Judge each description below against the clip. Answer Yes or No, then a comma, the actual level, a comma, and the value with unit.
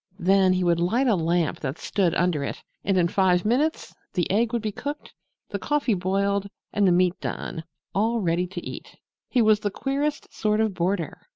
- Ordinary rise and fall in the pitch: Yes, average, 3.8 semitones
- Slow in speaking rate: No, average, 195 wpm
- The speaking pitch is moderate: No, high, 195 Hz